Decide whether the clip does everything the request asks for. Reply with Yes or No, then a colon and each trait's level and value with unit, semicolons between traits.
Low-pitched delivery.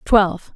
No: high, 200 Hz